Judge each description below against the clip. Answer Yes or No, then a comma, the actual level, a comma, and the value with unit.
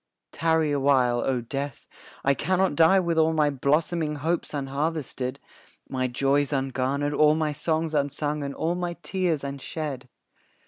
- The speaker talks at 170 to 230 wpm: No, average, 145 wpm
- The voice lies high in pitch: No, medium, 145 Hz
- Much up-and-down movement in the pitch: No, average, 2.7 semitones